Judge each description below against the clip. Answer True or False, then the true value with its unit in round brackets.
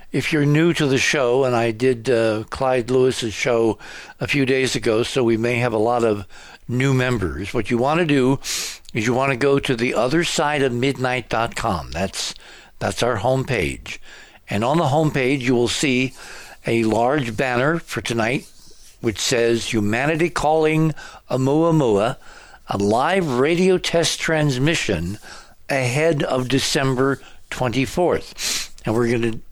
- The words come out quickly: False (155 wpm)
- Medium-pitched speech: False (130 Hz)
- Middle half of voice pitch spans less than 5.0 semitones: True (3.4 semitones)